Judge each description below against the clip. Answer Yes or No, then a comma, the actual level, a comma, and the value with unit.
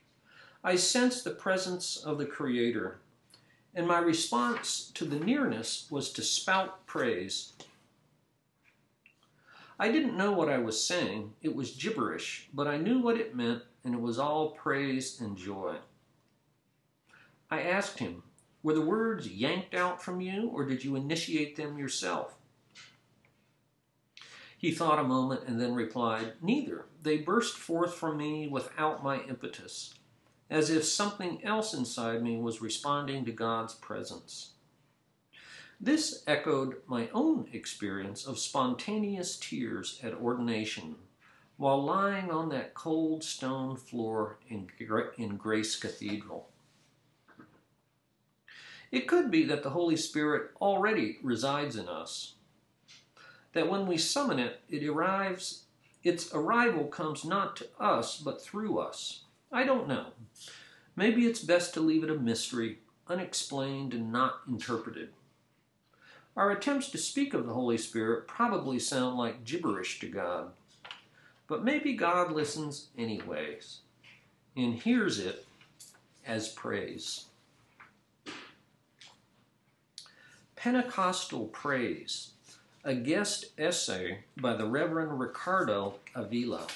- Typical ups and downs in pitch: No, wide, 7.8 semitones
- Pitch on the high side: No, medium, 150 Hz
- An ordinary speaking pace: No, slow, 125 wpm